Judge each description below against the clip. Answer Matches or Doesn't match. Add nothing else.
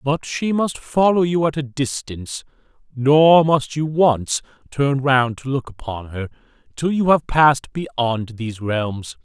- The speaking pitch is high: Doesn't match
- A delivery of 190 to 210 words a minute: Doesn't match